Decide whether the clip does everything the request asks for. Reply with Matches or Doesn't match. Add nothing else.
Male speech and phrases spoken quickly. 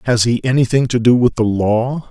Matches